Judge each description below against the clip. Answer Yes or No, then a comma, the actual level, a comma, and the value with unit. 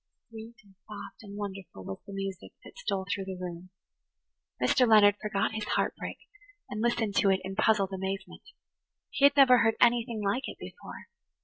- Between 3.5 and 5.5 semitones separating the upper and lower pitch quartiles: No, average, 2.7 semitones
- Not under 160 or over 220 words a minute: Yes, average, 180 wpm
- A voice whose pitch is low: No, high, 205 Hz